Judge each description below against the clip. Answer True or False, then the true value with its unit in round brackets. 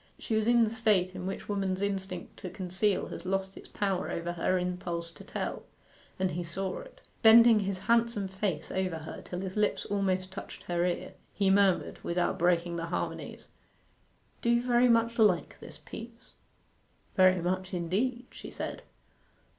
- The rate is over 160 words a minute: True (170 wpm)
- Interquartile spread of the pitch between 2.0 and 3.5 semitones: True (3.2 semitones)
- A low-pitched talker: False (190 Hz)